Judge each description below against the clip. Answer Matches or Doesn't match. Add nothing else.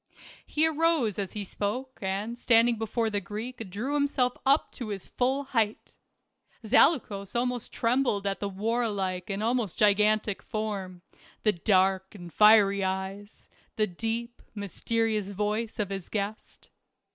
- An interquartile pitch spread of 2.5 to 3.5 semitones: Matches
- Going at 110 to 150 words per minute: Matches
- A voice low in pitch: Doesn't match